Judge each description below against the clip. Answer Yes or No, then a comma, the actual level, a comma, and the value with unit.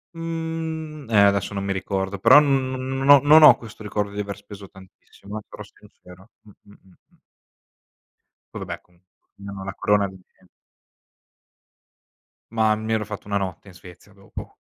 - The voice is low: Yes, low, 105 Hz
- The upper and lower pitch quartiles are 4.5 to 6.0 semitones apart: Yes, average, 5.0 semitones